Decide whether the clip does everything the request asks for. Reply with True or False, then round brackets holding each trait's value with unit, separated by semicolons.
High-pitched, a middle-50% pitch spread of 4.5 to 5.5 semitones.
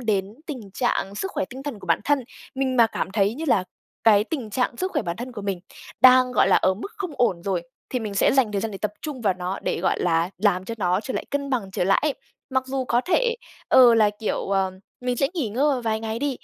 True (225 Hz; 5.0 semitones)